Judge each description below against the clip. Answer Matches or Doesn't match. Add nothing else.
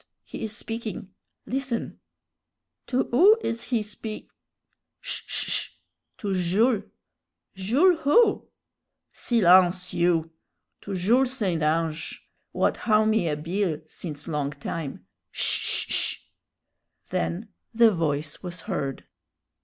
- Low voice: Doesn't match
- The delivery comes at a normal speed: Doesn't match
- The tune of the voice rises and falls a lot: Matches